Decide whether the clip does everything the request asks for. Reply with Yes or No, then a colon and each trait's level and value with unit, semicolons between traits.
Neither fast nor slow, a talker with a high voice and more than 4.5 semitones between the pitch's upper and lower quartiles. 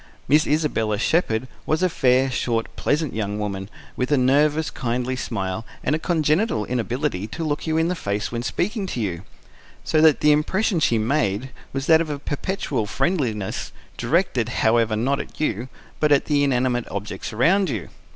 No: average, 175 wpm; low, 130 Hz; wide, 5.6 semitones